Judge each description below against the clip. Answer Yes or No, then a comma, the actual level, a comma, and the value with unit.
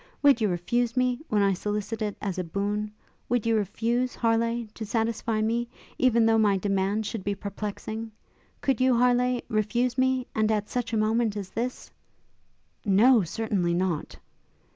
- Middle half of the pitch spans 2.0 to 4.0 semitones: Yes, average, 2.7 semitones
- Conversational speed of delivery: Yes, average, 165 wpm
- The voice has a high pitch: Yes, high, 220 Hz